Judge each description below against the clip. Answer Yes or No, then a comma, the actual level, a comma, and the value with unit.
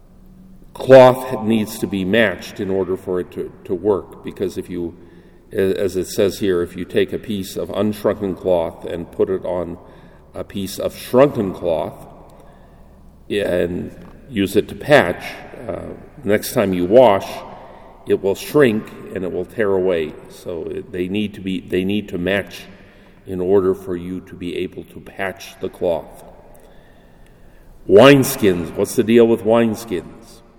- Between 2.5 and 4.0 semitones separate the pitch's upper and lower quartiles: Yes, average, 3.3 semitones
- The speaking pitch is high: No, very low, 95 Hz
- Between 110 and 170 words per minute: Yes, average, 155 wpm